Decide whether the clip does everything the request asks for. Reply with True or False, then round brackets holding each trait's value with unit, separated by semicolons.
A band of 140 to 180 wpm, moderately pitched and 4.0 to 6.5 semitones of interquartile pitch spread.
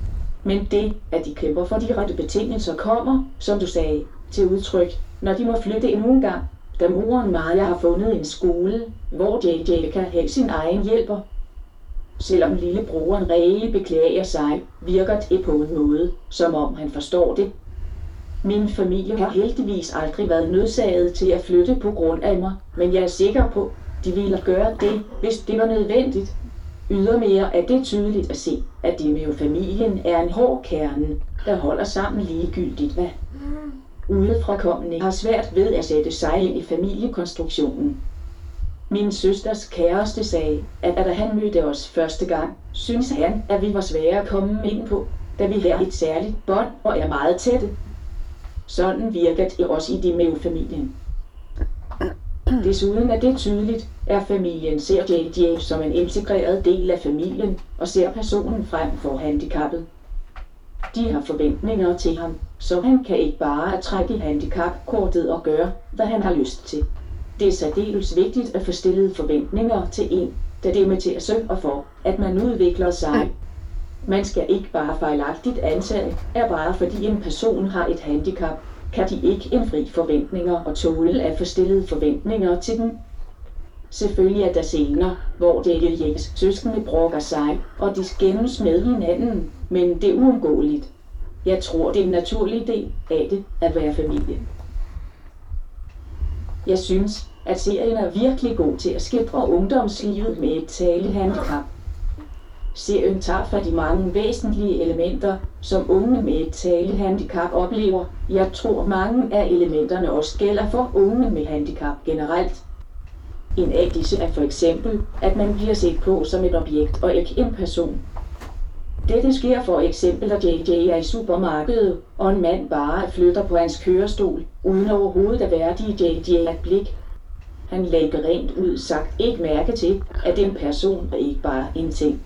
True (165 wpm; 180 Hz; 4.5 semitones)